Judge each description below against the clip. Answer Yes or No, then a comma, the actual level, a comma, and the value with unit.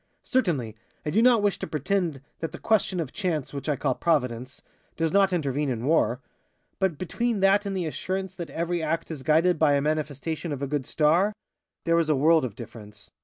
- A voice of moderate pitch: Yes, medium, 160 Hz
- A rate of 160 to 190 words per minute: No, fast, 205 wpm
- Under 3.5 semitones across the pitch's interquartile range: No, average, 4.8 semitones